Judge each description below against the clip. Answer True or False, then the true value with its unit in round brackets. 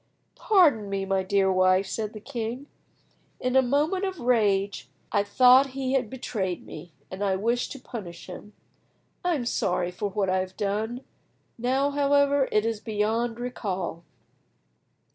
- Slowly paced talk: False (155 wpm)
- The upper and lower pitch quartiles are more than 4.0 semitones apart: True (5.1 semitones)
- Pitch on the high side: True (220 Hz)